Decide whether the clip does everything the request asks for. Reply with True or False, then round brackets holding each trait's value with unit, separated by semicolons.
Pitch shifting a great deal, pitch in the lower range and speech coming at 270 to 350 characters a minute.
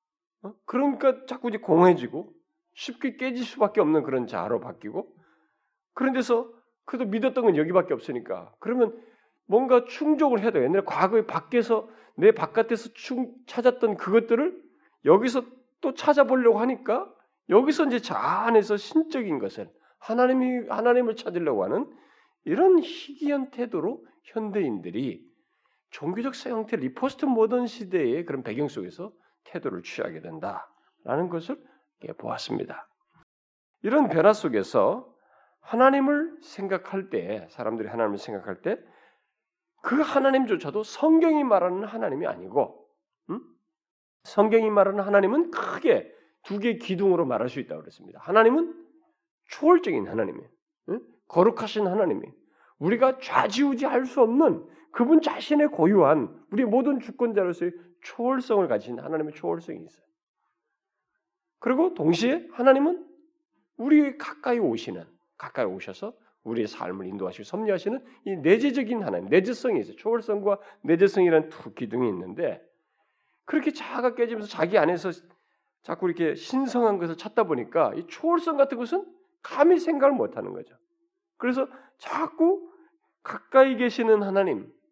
False (6.3 semitones; 250 Hz; 315 characters per minute)